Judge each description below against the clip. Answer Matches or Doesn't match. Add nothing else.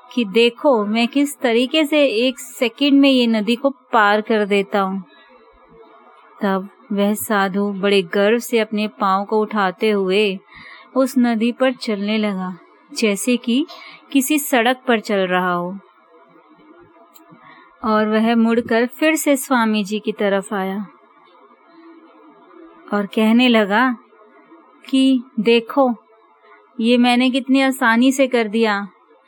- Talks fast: Doesn't match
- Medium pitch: Doesn't match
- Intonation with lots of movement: Doesn't match